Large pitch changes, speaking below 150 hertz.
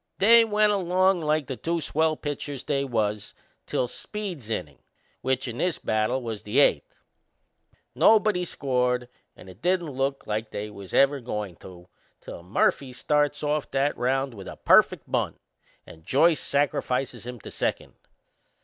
Yes: wide, 6.0 semitones; low, 135 Hz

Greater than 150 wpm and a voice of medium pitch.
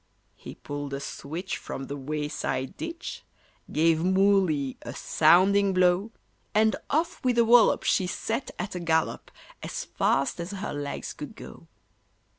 No: average, 145 wpm; medium, 180 Hz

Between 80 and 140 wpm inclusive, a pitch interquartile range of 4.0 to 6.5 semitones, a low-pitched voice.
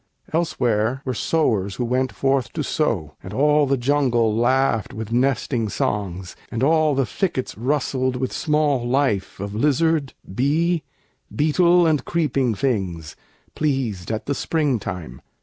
Yes: slow, 135 wpm; average, 5.2 semitones; low, 130 Hz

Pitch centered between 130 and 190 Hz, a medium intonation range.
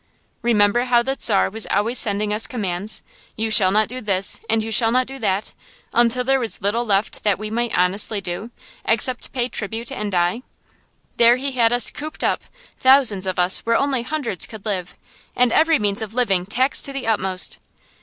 No: high, 225 Hz; average, 3.4 semitones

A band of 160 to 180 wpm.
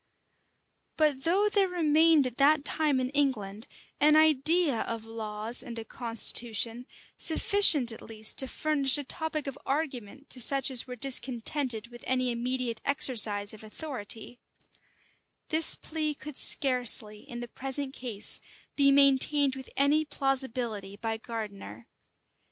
No: average, 140 wpm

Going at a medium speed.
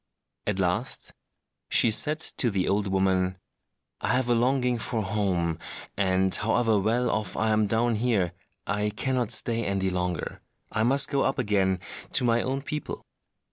Yes: average, 160 wpm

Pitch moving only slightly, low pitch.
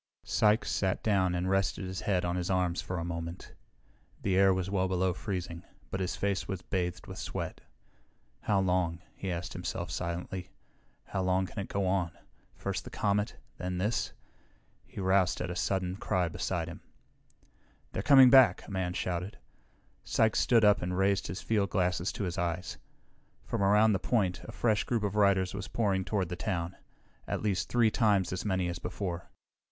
Yes: narrow, 2.0 semitones; very low, 95 Hz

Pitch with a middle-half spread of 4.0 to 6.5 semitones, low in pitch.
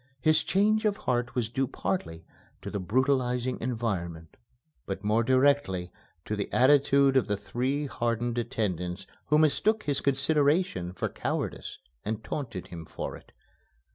Yes: wide, 5.5 semitones; low, 125 Hz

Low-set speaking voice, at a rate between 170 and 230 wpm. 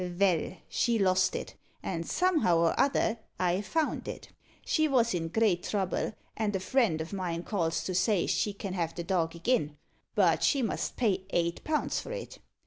No: high, 190 Hz; average, 180 wpm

